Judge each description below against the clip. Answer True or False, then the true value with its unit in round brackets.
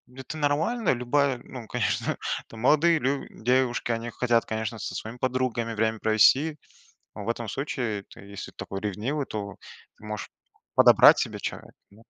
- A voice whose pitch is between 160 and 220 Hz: False (120 Hz)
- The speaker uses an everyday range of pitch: True (3.7 semitones)